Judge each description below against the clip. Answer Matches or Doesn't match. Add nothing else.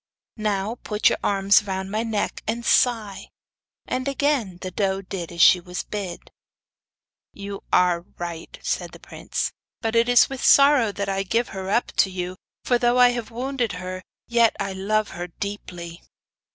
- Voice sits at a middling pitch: Doesn't match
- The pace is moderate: Matches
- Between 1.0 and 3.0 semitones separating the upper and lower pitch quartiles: Doesn't match